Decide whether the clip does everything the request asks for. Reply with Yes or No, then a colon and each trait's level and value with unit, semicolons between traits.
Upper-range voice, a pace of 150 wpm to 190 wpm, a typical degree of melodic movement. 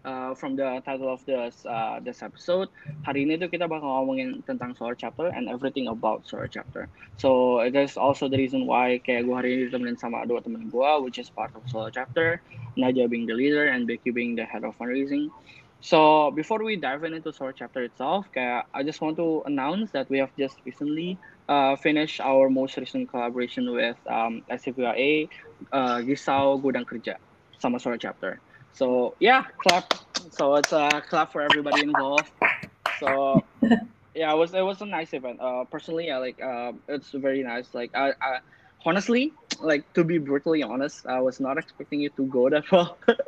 No: low, 135 Hz; fast, 175 wpm; average, 4.0 semitones